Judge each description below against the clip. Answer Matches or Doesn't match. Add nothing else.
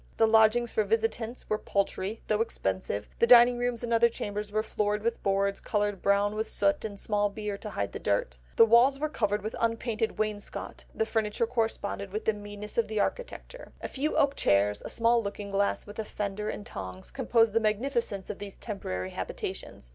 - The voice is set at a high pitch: Matches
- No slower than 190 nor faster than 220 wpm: Matches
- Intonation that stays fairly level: Matches